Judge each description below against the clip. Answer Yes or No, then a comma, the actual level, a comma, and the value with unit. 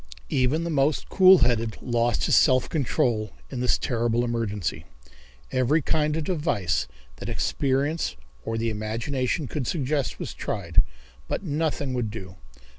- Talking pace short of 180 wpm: Yes, average, 140 wpm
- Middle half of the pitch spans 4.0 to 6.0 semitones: Yes, average, 4.6 semitones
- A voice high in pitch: No, low, 125 Hz